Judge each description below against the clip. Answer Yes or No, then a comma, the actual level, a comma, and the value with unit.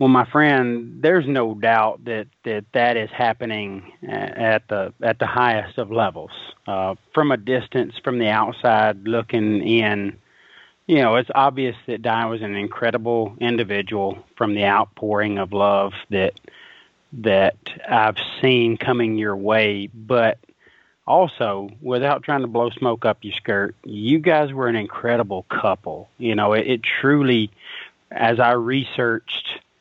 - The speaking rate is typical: Yes, average, 145 wpm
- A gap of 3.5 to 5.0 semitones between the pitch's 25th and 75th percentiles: No, average, 2.8 semitones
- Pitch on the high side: No, low, 115 Hz